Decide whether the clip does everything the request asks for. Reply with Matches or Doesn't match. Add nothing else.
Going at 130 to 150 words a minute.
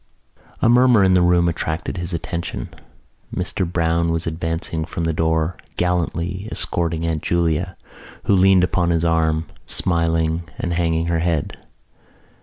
Matches